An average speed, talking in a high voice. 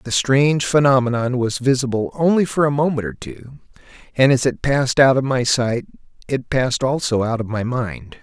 No: average, 190 wpm; low, 130 Hz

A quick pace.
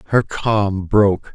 No: slow, 135 wpm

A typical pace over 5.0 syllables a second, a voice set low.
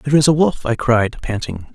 Yes: 5.4 syllables/s; low, 125 Hz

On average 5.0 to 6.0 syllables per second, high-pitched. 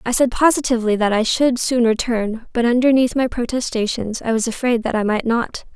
Yes: 5.4 syllables/s; high, 235 Hz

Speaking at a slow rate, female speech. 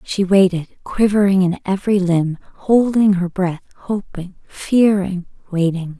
Yes: slow, 110 wpm; female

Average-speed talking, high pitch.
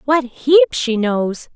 Yes: average, 155 wpm; very high, 250 Hz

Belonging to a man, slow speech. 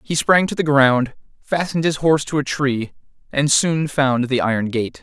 No: male; fast, 205 wpm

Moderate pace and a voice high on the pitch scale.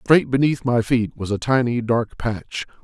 No: average, 190 wpm; low, 120 Hz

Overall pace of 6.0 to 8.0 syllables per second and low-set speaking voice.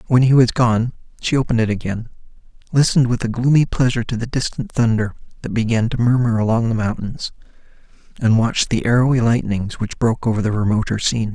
Yes: 6.3 syllables/s; low, 115 Hz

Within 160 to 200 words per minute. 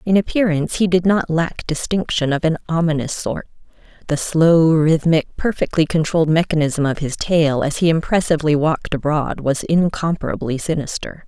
No: average, 150 wpm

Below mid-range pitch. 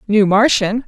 No: high, 215 Hz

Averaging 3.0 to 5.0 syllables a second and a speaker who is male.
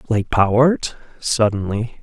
Yes: 3.9 syllables/s; male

